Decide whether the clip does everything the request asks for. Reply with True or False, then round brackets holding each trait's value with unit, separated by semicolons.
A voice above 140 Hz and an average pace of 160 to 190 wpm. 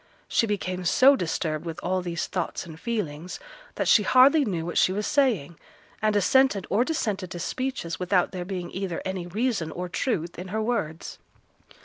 True (185 Hz; 175 wpm)